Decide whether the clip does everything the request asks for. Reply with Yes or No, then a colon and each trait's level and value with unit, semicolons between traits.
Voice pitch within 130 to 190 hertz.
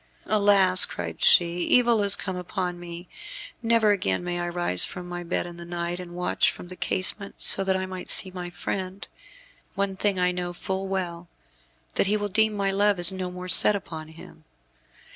Yes: medium, 185 Hz